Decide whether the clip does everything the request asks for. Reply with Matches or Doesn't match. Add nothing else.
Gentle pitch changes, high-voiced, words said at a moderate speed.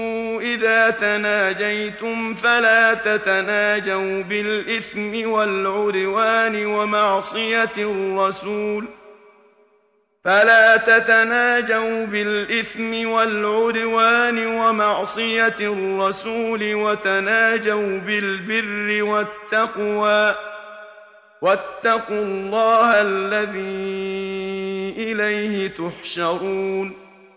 Doesn't match